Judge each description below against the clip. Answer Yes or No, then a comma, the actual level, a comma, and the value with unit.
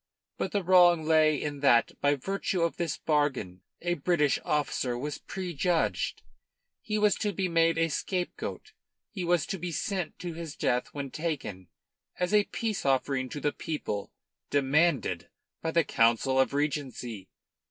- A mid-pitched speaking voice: Yes, medium, 155 Hz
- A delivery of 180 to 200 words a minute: No, average, 155 wpm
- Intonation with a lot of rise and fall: No, average, 4.3 semitones